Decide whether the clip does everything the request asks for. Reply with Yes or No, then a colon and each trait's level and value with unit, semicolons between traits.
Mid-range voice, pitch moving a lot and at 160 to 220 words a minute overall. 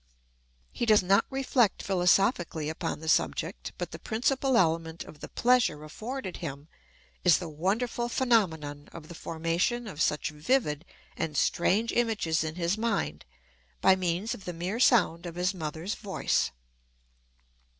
No: medium, 180 Hz; wide, 5.9 semitones; average, 145 wpm